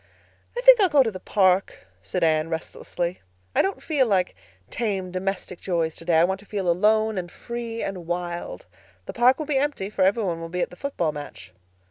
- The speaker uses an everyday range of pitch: Yes, average, 4.9 semitones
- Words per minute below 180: No, fast, 205 wpm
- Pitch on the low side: No, high, 190 Hz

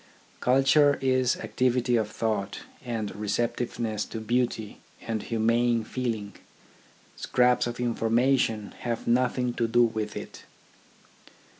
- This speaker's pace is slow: Yes, slow, 115 wpm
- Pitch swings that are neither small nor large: No, narrow, 2.1 semitones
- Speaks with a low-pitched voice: Yes, low, 120 Hz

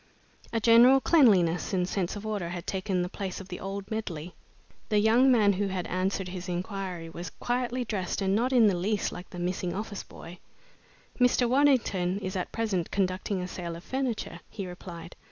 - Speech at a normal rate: Yes, average, 190 wpm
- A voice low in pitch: No, high, 195 Hz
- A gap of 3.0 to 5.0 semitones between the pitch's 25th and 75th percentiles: Yes, average, 3.6 semitones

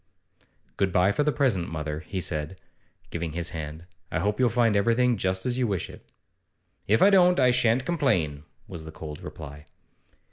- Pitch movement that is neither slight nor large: No, wide, 7.5 semitones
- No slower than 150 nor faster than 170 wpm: No, average, 180 wpm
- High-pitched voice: No, very low, 95 Hz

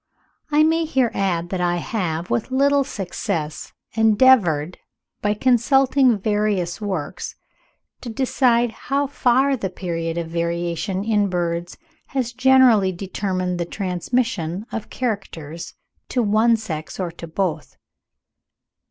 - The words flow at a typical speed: No, slow, 120 wpm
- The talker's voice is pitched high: Yes, high, 200 Hz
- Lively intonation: Yes, wide, 6.1 semitones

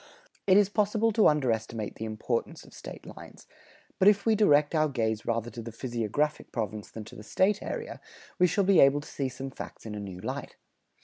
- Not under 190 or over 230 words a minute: Yes, fast, 205 wpm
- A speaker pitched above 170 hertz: No, low, 135 Hz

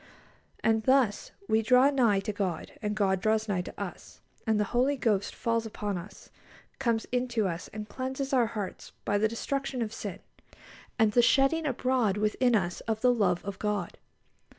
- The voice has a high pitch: Yes, high, 220 Hz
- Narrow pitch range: No, average, 3.5 semitones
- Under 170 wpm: No, average, 175 wpm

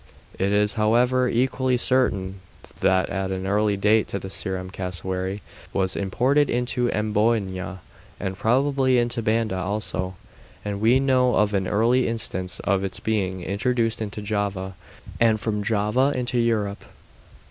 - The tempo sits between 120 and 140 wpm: Yes, slow, 135 wpm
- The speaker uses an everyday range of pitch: Yes, average, 3.9 semitones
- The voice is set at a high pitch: No, low, 105 Hz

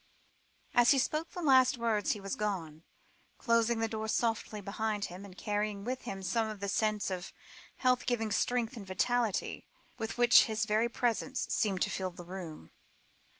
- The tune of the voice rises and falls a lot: No, average, 3.1 semitones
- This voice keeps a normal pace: Yes, average, 175 wpm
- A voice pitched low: No, high, 220 Hz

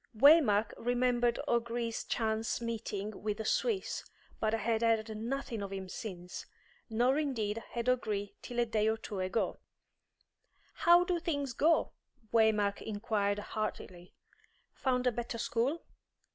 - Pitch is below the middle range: No, high, 225 Hz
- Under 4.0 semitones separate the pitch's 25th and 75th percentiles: Yes, average, 2.7 semitones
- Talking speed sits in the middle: No, slow, 130 wpm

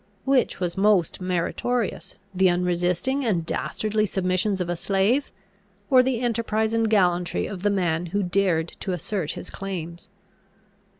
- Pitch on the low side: No, high, 190 Hz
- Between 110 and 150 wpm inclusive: Yes, average, 140 wpm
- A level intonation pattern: No, average, 3.6 semitones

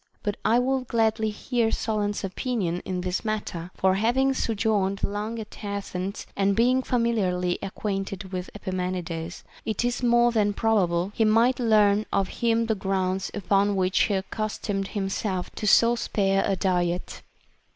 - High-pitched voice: Yes, high, 205 Hz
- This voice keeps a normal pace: Yes, average, 150 wpm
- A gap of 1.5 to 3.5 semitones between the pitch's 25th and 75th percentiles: Yes, average, 3.0 semitones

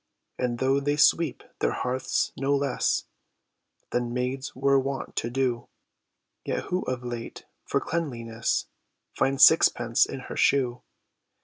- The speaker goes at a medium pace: No, slow, 130 wpm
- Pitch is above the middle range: No, low, 130 Hz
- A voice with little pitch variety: Yes, narrow, 2.3 semitones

